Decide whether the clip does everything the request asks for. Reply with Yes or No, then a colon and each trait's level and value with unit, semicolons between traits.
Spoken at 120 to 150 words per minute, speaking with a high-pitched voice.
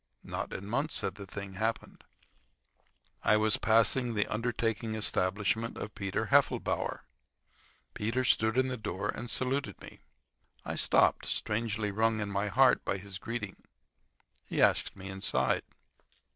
No: average, 140 wpm; low, 110 Hz